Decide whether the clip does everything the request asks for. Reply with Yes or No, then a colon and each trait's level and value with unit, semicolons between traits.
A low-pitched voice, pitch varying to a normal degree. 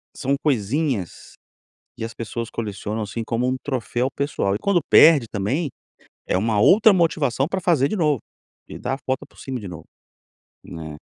No: low, 130 Hz; wide, 5.7 semitones